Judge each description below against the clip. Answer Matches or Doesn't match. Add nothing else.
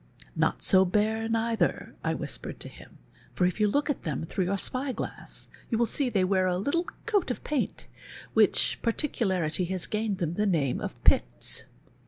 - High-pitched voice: Matches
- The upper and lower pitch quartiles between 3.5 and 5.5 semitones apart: Matches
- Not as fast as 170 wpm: Doesn't match